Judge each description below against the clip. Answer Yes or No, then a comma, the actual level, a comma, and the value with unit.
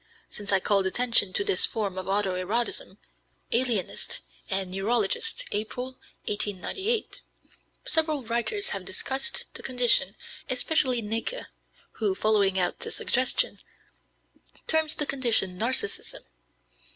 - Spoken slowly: Yes, slow, 115 wpm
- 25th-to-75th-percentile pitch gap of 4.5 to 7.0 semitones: Yes, wide, 5.4 semitones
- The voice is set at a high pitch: Yes, high, 230 Hz